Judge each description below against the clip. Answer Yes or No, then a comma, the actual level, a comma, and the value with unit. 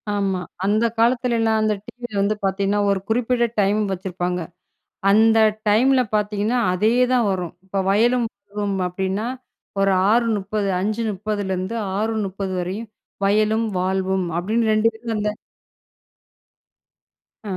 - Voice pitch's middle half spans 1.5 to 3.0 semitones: Yes, narrow, 2.5 semitones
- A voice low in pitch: No, high, 210 Hz